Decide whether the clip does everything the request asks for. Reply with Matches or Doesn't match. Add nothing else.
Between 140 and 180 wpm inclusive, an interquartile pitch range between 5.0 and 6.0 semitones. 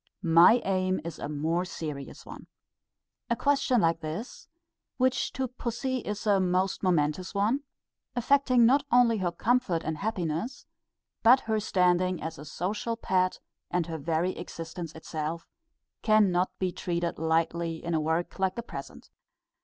Matches